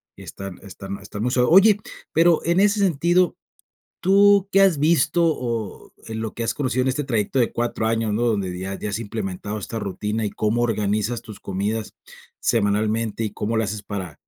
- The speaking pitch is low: Yes, low, 115 Hz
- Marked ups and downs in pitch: Yes, wide, 6.0 semitones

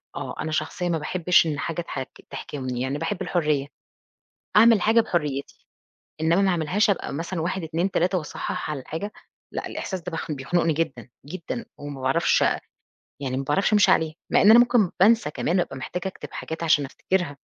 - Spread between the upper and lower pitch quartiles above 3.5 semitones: Yes, average, 4.3 semitones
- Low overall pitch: No, medium, 165 Hz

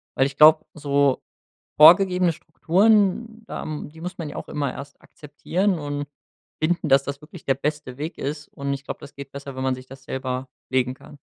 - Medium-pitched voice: Yes, medium, 145 Hz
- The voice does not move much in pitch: No, average, 3.3 semitones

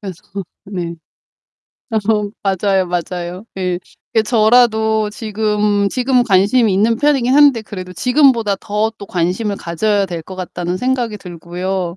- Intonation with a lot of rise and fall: No, average, 3.5 semitones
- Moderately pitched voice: No, high, 205 Hz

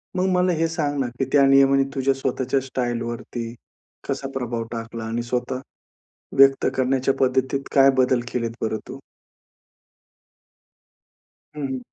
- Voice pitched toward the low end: Yes, low, 130 Hz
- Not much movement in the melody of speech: Yes, narrow, 2.2 semitones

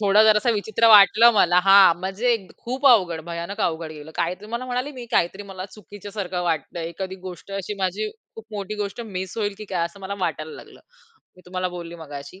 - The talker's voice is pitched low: No, high, 190 Hz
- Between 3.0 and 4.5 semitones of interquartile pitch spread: Yes, average, 3.6 semitones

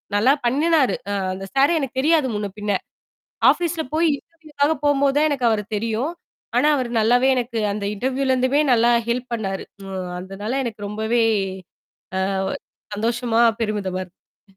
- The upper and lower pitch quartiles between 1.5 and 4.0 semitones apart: No, average, 4.7 semitones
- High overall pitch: Yes, high, 240 Hz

